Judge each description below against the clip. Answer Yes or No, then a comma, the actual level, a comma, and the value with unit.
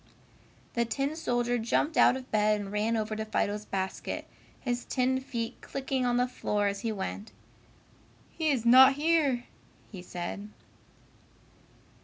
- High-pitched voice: Yes, high, 235 Hz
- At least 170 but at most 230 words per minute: No, average, 145 wpm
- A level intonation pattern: No, average, 3.8 semitones